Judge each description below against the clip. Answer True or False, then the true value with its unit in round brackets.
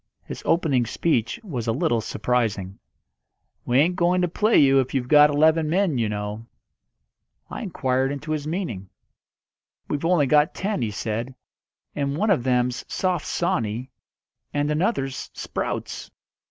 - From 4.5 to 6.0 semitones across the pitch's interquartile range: True (5.5 semitones)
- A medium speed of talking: True (145 wpm)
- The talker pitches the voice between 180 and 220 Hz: False (140 Hz)